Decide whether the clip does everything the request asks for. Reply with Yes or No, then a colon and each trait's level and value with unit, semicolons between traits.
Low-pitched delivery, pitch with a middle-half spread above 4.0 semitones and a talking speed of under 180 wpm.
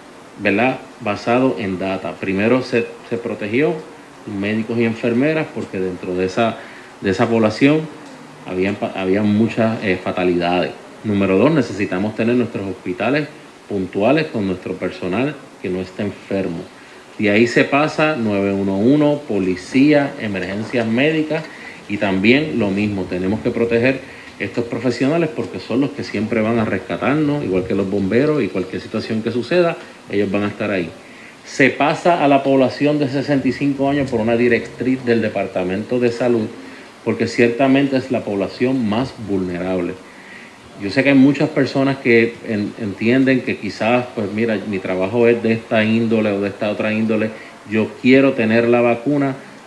Yes: low, 115 Hz; average, 4.7 semitones; average, 150 wpm